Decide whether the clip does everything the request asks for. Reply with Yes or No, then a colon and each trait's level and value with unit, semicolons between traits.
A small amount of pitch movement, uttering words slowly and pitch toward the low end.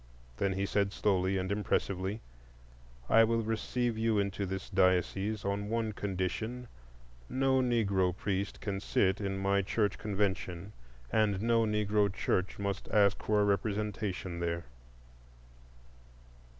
Yes: narrow, 2.1 semitones; slow, 125 wpm; low, 100 Hz